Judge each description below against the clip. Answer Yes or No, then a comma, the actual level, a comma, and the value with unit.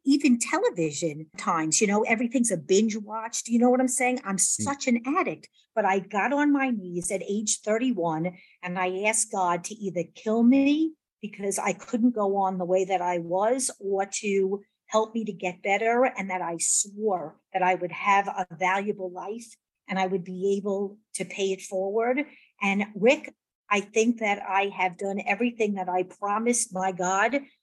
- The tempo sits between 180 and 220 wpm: Yes, average, 190 wpm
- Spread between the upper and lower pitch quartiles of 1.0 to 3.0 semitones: No, average, 3.7 semitones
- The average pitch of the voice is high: Yes, high, 200 Hz